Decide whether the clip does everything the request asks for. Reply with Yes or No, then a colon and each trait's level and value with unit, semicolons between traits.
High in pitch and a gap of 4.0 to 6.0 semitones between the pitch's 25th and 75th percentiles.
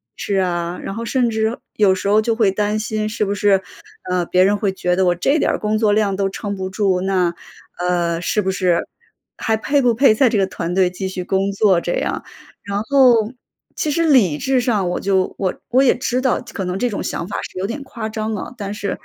No: high, 200 Hz; average, 3.0 semitones